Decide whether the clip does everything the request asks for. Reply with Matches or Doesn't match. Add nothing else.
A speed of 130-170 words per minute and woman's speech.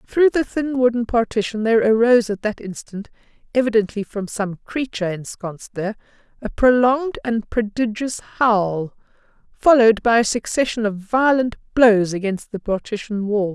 Matches